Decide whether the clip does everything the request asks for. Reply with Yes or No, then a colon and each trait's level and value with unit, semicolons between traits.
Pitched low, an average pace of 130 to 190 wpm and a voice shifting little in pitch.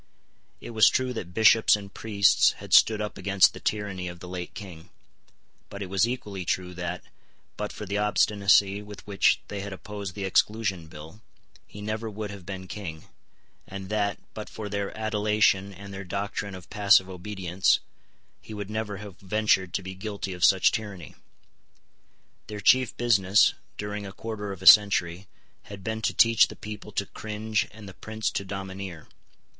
Yes: low, 100 Hz; average, 175 wpm; narrow, 2.0 semitones